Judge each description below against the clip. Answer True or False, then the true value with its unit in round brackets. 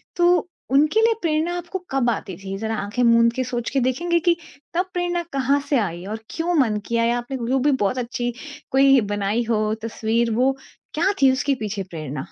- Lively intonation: True (5.7 semitones)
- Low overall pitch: False (250 Hz)